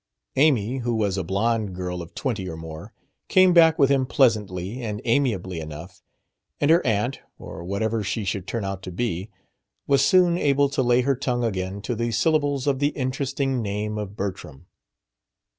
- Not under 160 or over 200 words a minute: Yes, average, 175 wpm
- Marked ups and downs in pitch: Yes, wide, 6.0 semitones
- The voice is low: Yes, low, 115 Hz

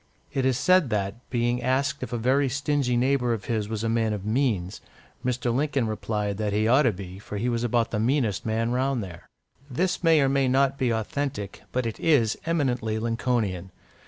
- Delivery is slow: No, average, 200 wpm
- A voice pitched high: No, low, 120 Hz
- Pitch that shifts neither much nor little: Yes, average, 3.6 semitones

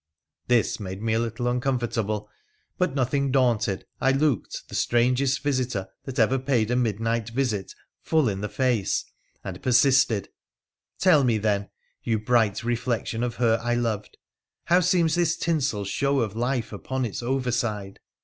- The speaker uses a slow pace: No, average, 160 wpm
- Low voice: Yes, low, 120 Hz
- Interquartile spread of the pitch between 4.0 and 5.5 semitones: No, average, 3.3 semitones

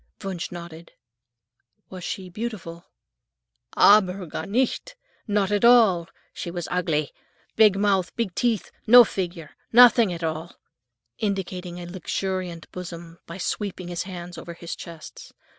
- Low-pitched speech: No, medium, 180 Hz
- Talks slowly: Yes, slow, 130 wpm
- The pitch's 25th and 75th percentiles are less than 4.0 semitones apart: Yes, average, 3.1 semitones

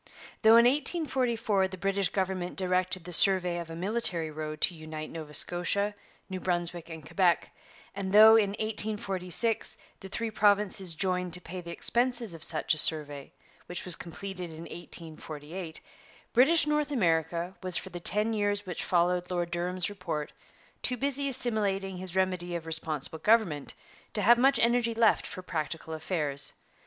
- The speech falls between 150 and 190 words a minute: Yes, average, 160 wpm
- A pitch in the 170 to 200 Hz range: Yes, medium, 185 Hz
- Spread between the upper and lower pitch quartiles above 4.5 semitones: No, average, 3.9 semitones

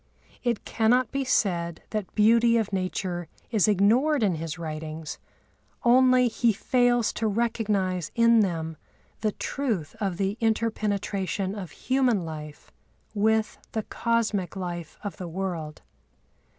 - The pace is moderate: No, slow, 130 wpm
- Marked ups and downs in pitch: No, average, 4.7 semitones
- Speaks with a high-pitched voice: Yes, high, 205 Hz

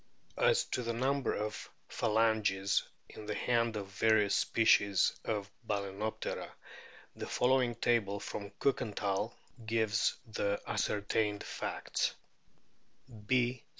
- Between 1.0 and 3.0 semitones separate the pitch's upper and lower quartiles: Yes, narrow, 2.5 semitones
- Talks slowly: Yes, slow, 115 wpm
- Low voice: Yes, low, 110 Hz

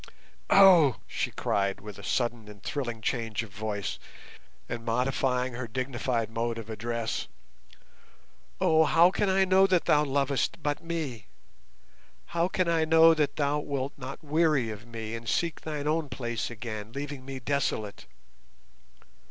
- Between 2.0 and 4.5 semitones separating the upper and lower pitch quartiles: No, average, 5.2 semitones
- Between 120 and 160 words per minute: Yes, average, 150 wpm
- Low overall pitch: Yes, low, 130 Hz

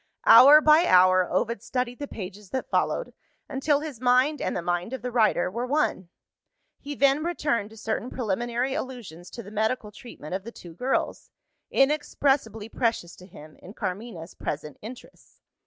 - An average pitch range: No, wide, 6.0 semitones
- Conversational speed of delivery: Yes, average, 165 wpm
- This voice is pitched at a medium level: No, high, 235 Hz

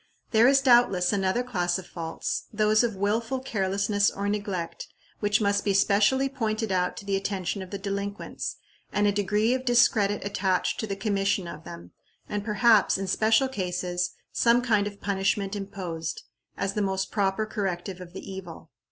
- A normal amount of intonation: No, narrow, 2.2 semitones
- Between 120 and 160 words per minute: No, average, 170 wpm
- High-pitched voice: Yes, high, 200 Hz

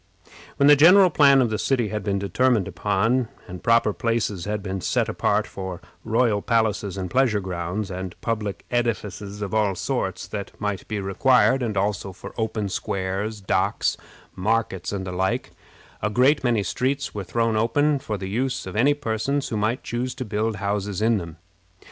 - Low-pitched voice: Yes, low, 105 Hz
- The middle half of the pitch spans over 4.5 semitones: No, average, 3.7 semitones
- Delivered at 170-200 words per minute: Yes, average, 180 wpm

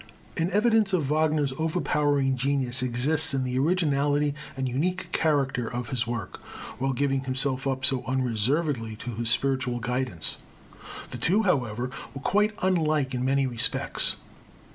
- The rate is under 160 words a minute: Yes, average, 140 wpm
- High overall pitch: No, low, 135 Hz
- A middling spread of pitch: Yes, average, 3.5 semitones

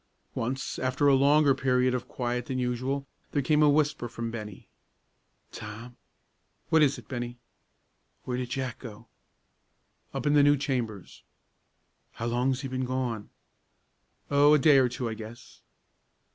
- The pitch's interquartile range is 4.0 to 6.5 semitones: No, average, 2.7 semitones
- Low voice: Yes, low, 130 Hz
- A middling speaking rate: Yes, average, 150 wpm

